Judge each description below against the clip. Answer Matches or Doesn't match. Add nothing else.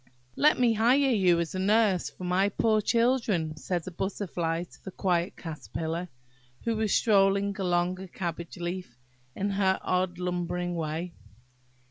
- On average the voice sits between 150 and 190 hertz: Matches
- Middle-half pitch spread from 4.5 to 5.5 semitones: Doesn't match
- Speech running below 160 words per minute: Matches